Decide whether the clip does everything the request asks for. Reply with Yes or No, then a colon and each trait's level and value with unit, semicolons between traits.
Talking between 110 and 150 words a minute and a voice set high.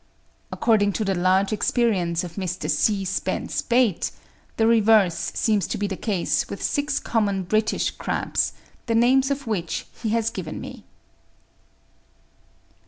Yes: average, 140 wpm; high, 210 Hz